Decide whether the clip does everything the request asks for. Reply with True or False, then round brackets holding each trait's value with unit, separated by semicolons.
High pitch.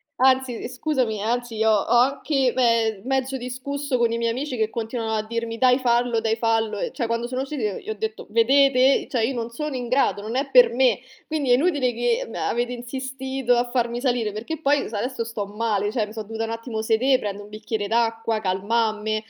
True (235 Hz)